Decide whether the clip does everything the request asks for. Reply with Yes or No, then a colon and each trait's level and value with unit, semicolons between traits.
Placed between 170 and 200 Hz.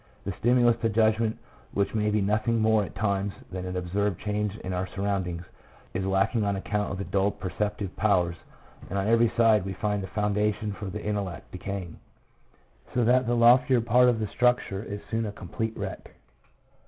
No: low, 105 Hz